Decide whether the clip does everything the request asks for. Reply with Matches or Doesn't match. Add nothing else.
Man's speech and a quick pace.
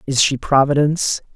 Doesn't match